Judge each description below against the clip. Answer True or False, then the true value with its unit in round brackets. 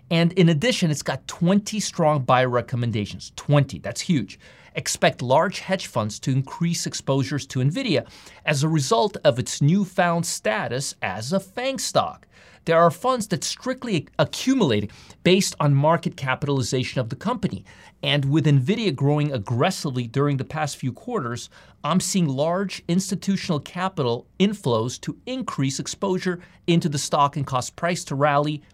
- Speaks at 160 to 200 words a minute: False (150 wpm)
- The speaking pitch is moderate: True (155 Hz)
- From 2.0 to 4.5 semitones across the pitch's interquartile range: False (5.6 semitones)